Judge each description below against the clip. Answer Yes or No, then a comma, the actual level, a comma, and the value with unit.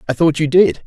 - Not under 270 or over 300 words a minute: Yes, fast, 275 wpm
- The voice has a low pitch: No, medium, 150 Hz